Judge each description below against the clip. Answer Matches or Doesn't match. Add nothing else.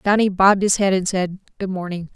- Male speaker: Doesn't match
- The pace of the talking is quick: Matches